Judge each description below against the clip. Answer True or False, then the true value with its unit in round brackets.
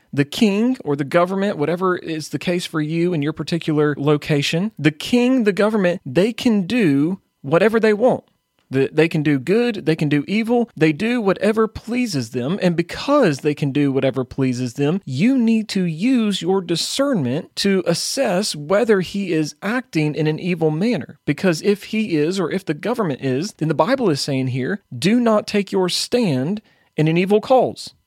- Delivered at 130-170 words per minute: False (185 wpm)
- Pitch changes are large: True (5.9 semitones)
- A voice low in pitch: False (180 Hz)